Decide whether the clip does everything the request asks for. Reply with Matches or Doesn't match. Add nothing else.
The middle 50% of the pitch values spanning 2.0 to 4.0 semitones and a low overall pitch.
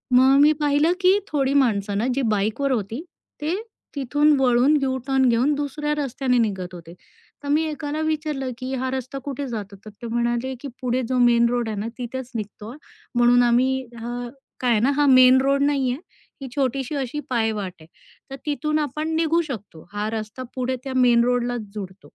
Doesn't match